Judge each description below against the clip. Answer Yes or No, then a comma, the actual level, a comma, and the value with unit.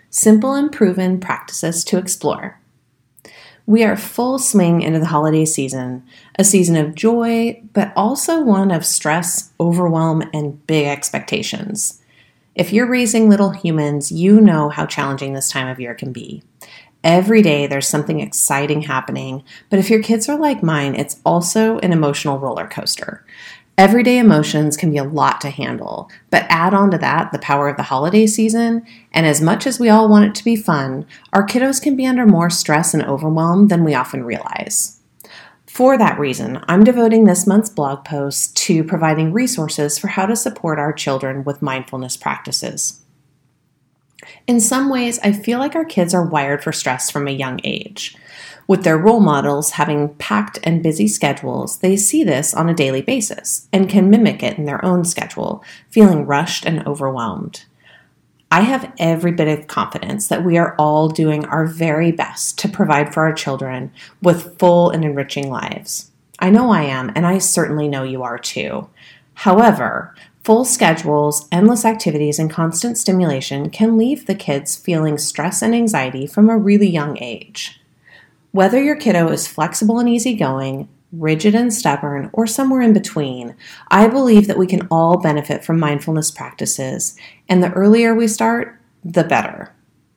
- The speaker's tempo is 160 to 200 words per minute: Yes, average, 170 wpm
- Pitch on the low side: No, medium, 170 Hz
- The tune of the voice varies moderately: No, wide, 6.3 semitones